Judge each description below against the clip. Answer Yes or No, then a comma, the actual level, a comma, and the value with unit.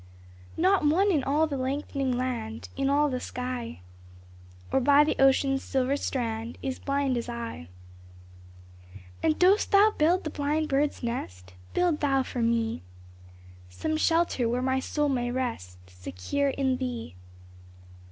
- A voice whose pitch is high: Yes, very high, 265 Hz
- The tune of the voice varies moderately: Yes, average, 3.5 semitones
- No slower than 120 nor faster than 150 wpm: Yes, average, 140 wpm